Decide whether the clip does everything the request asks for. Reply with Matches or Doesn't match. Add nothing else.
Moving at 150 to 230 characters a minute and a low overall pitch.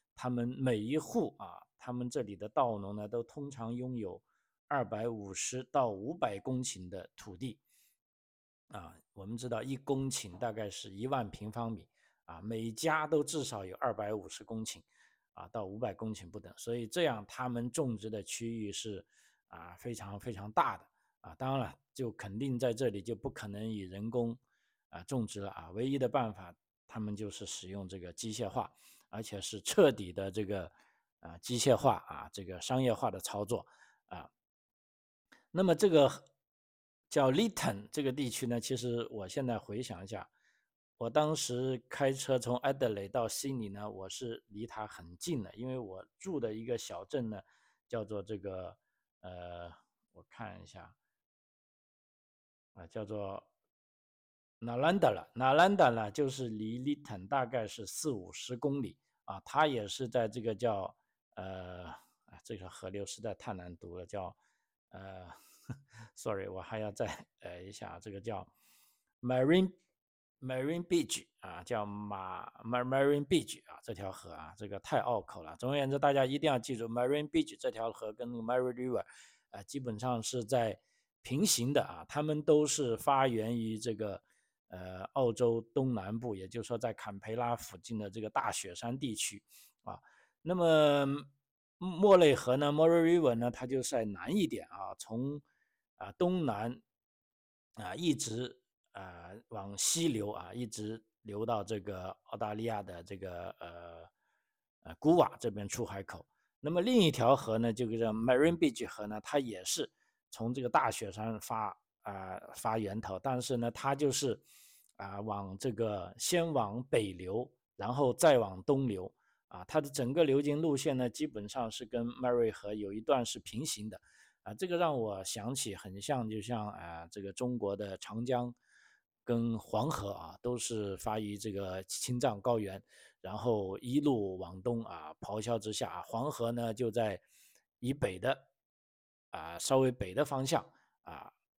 Doesn't match